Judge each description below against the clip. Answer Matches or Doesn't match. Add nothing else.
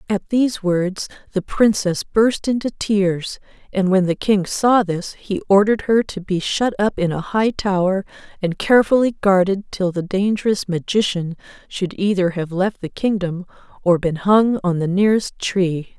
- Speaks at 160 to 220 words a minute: Matches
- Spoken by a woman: Matches